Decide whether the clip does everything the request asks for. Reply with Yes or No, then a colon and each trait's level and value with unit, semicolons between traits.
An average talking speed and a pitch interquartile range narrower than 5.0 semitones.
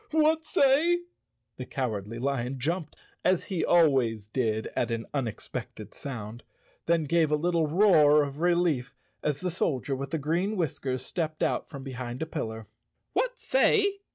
No: average, 155 wpm; wide, 5.6 semitones